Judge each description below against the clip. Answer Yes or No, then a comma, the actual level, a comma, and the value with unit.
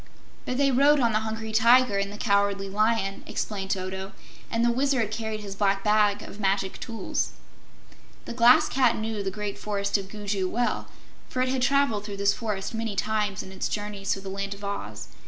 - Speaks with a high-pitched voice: Yes, high, 210 Hz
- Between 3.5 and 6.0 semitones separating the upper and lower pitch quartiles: No, narrow, 2.5 semitones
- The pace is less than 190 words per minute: No, average, 195 wpm